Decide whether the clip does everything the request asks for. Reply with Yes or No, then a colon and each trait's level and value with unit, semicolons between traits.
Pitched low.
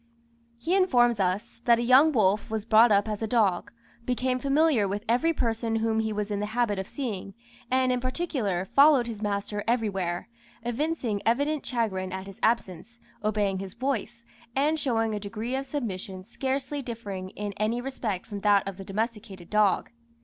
No: high, 225 Hz